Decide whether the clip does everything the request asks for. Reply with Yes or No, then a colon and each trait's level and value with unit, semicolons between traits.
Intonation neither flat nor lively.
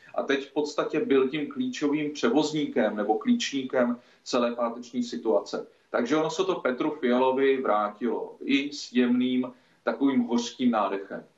Yes: average, 3.9 semitones